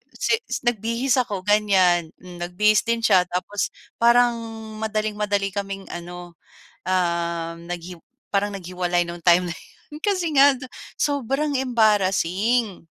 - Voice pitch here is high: Yes, high, 200 Hz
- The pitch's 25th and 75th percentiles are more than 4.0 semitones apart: Yes, average, 4.8 semitones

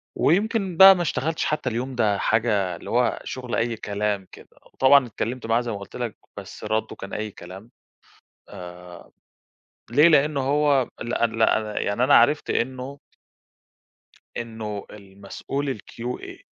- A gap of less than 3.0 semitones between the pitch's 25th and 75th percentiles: No, average, 4.8 semitones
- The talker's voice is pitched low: Yes, low, 120 Hz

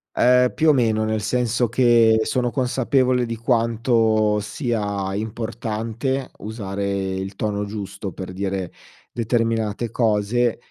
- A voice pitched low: Yes, low, 110 Hz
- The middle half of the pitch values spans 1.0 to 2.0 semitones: No, average, 2.7 semitones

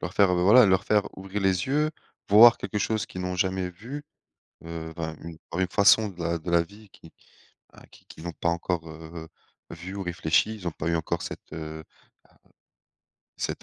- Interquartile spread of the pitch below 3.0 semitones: No, average, 3.4 semitones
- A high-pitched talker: No, very low, 90 Hz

